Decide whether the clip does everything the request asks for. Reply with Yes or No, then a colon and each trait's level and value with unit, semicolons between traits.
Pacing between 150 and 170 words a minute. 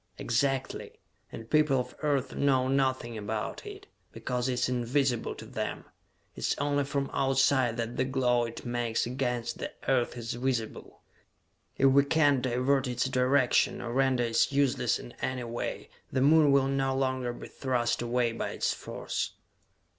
Yes: average, 160 wpm